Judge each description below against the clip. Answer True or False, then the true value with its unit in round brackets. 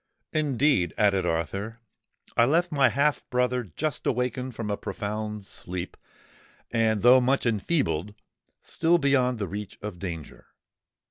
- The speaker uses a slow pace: True (130 wpm)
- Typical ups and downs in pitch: True (4.6 semitones)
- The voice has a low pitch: True (115 Hz)